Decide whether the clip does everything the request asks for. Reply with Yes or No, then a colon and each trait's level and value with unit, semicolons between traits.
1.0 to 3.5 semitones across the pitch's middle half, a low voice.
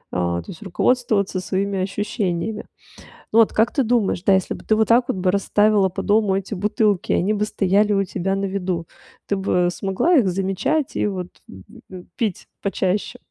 No: narrow, 2.4 semitones; high, 195 Hz